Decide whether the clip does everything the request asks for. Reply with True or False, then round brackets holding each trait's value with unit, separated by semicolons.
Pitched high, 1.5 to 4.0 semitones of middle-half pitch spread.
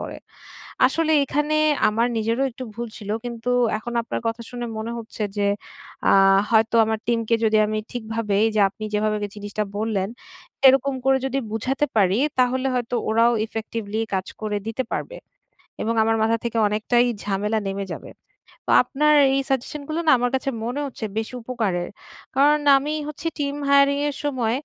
True (230 Hz; 3.6 semitones)